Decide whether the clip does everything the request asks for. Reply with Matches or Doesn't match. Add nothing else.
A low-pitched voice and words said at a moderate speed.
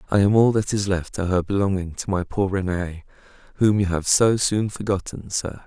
Doesn't match